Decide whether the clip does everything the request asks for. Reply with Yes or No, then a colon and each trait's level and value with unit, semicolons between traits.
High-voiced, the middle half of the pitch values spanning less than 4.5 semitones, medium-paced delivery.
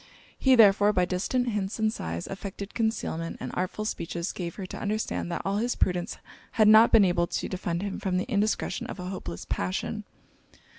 Yes: high, 195 Hz; average, 3.3 semitones; average, 190 wpm